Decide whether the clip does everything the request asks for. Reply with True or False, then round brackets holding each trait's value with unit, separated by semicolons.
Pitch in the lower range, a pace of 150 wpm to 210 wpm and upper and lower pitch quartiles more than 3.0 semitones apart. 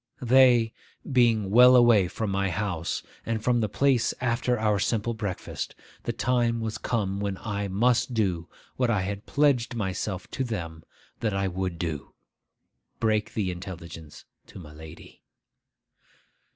False (105 Hz; 140 wpm; 3.9 semitones)